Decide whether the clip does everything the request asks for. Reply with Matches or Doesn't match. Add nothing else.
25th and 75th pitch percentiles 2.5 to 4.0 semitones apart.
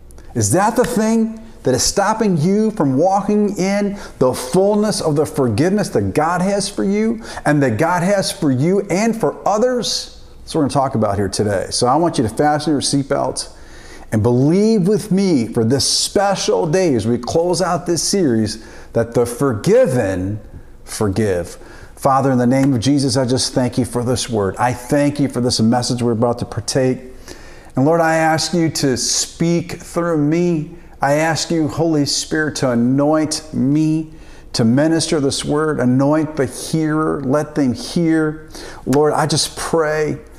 Doesn't match